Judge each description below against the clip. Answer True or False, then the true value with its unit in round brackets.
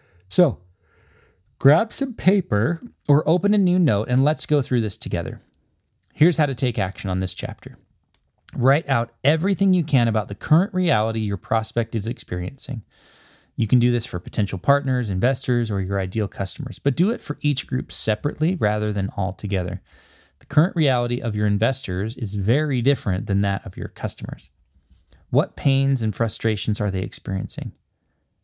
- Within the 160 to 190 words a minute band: True (170 wpm)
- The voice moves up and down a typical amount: False (6.1 semitones)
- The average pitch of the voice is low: True (115 Hz)